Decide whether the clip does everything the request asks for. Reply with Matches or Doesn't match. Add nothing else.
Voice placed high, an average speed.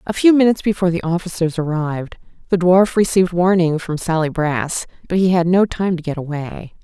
Doesn't match